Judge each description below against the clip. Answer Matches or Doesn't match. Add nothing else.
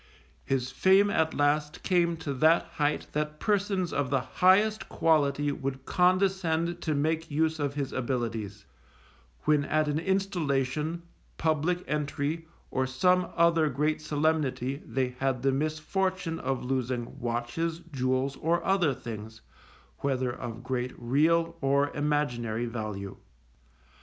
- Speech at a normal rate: Doesn't match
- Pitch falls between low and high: Matches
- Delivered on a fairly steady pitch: Doesn't match